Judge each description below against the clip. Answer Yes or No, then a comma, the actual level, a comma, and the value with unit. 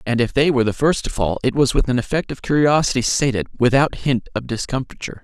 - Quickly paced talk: Yes, fast, 230 wpm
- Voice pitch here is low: Yes, low, 130 Hz